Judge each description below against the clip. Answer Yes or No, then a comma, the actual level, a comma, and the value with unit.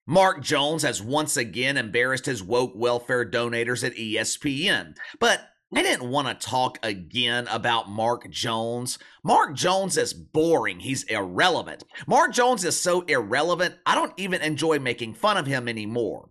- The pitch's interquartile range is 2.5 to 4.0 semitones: No, average, 4.7 semitones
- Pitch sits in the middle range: No, low, 125 Hz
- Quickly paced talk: No, average, 155 wpm